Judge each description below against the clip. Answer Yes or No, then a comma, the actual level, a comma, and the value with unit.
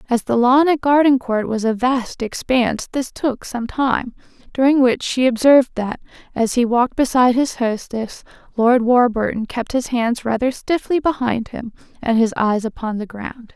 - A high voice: Yes, high, 245 Hz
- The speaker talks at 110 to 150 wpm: No, average, 175 wpm